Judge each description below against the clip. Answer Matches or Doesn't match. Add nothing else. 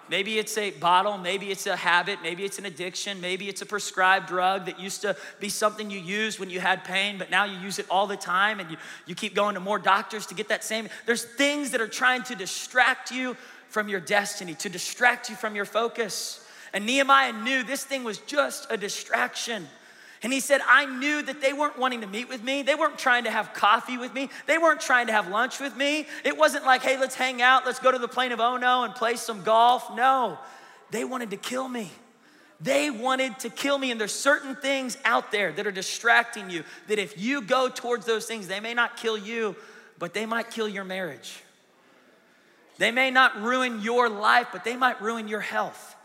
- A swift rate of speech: Matches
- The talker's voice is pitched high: Matches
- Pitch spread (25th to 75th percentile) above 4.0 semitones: Matches